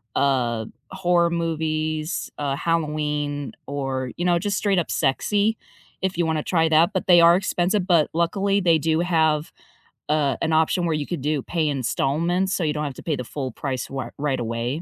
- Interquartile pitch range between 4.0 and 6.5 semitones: No, average, 3.3 semitones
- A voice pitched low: No, medium, 160 Hz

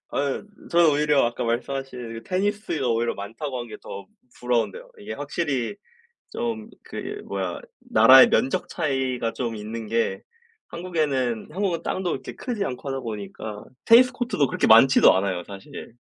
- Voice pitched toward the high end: No, low, 135 Hz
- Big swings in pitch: Yes, wide, 6.8 semitones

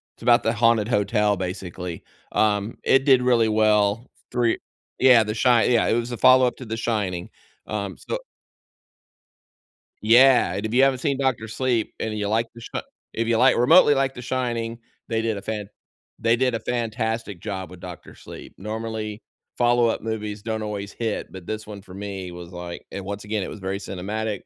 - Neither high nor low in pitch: No, low, 110 Hz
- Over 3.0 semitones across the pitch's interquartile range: No, average, 2.7 semitones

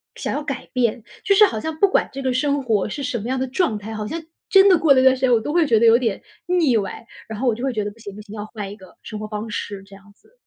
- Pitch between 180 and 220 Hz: No, high, 240 Hz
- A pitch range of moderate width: Yes, average, 5.0 semitones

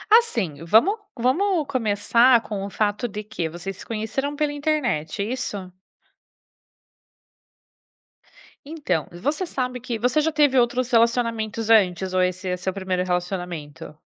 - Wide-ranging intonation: Yes, wide, 5.9 semitones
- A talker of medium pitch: No, high, 220 Hz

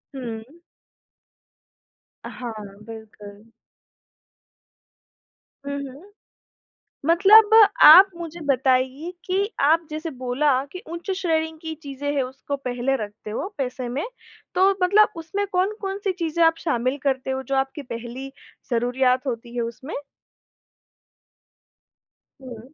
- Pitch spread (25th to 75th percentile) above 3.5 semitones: Yes, average, 5.2 semitones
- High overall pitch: Yes, very high, 275 Hz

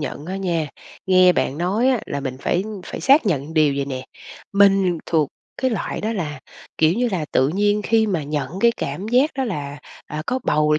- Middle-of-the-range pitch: Yes, medium, 175 Hz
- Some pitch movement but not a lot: No, wide, 6.0 semitones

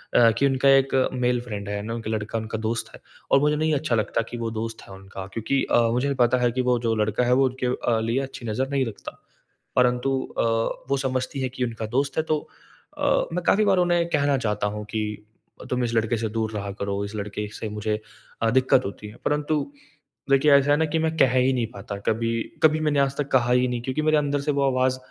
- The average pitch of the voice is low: Yes, low, 125 Hz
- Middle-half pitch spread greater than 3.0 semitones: Yes, average, 3.8 semitones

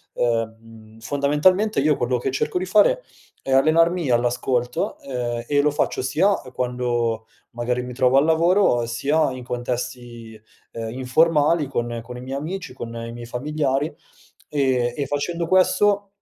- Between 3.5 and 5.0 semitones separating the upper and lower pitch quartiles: Yes, average, 4.4 semitones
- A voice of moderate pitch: No, low, 130 Hz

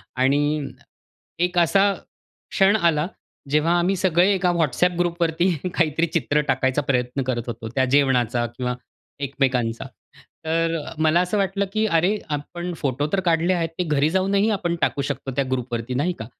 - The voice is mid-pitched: Yes, medium, 160 Hz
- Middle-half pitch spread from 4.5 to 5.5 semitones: Yes, average, 4.9 semitones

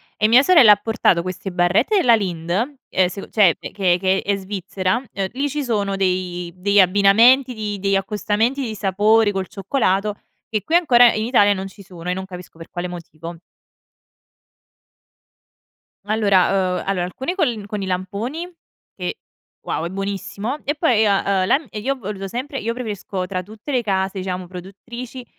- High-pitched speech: Yes, high, 200 Hz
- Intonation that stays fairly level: No, average, 3.8 semitones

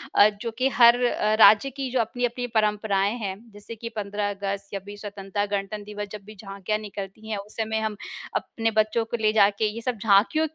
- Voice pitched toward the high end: Yes, high, 210 Hz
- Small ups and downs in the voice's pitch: Yes, narrow, 1.9 semitones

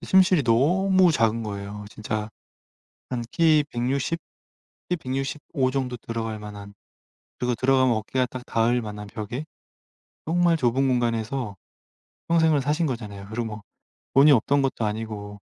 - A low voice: Yes, low, 125 Hz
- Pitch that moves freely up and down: No, average, 4.5 semitones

